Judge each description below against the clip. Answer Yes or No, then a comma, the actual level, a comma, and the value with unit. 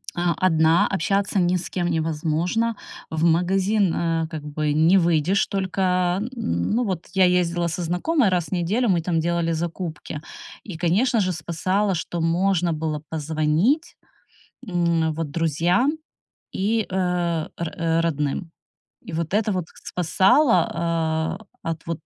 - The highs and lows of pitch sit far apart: No, average, 2.7 semitones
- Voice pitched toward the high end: No, medium, 170 Hz